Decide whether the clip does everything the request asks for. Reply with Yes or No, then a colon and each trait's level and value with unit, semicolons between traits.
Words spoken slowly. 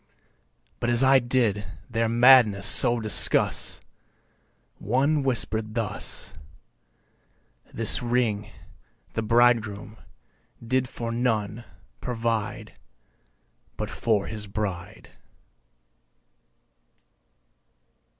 Yes: slow, 75 wpm